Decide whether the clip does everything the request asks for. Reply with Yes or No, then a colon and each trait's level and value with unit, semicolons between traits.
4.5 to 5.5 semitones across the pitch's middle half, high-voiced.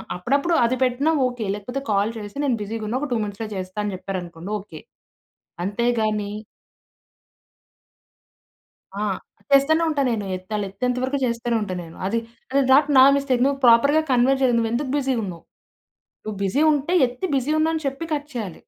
Yes: average, 5.0 semitones; high, 235 Hz